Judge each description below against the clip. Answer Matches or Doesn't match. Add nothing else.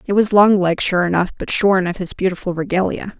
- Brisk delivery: Matches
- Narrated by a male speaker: Doesn't match